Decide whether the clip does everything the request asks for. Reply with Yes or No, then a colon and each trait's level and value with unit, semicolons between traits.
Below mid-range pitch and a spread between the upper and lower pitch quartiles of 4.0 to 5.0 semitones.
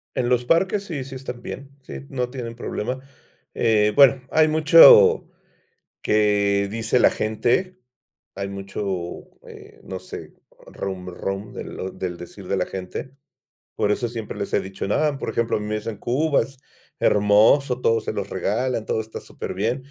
Yes: low, 115 Hz; average, 4.7 semitones